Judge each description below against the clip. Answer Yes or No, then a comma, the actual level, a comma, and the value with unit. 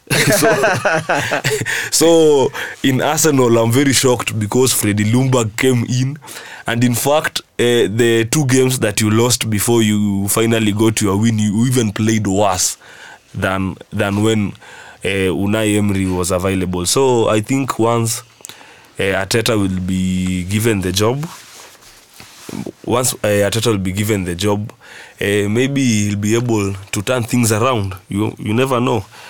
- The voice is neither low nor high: No, low, 110 Hz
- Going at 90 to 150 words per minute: Yes, average, 145 wpm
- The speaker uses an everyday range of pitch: Yes, average, 3.3 semitones